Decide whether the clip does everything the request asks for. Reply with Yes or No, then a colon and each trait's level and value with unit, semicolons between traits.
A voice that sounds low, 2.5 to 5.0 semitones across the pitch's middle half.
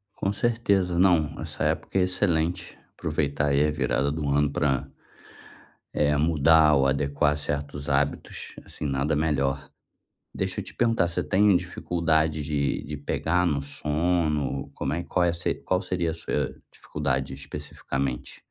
Yes: very low, 75 Hz; average, 3.3 semitones